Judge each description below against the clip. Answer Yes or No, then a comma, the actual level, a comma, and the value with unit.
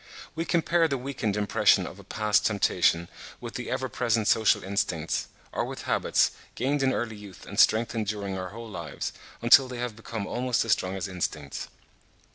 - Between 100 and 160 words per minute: No, average, 180 wpm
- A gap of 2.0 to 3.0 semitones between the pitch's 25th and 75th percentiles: No, average, 3.7 semitones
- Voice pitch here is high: No, low, 110 Hz